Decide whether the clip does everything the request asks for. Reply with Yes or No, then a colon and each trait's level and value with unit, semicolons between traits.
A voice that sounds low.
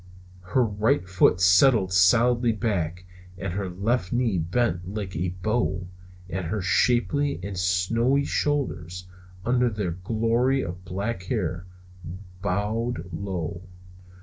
Yes: low, 100 Hz